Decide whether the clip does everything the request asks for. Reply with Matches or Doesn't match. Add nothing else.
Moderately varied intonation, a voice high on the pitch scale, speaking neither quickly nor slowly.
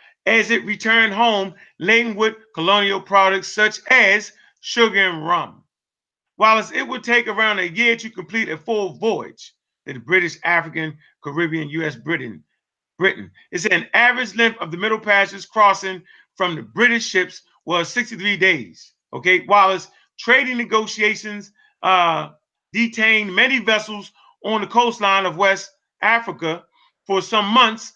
Matches